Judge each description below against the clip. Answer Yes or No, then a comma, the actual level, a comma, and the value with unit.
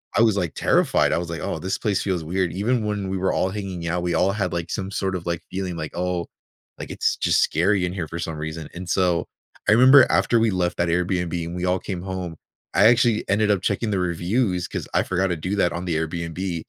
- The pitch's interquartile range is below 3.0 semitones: Yes, narrow, 2.4 semitones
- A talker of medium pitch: No, very low, 90 Hz